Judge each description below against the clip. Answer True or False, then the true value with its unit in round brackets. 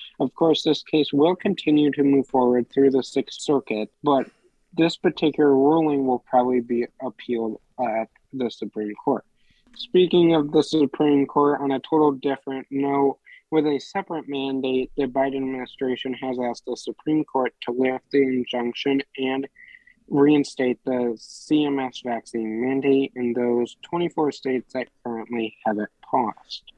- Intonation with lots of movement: False (3.1 semitones)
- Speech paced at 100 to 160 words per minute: True (150 wpm)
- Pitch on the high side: False (135 Hz)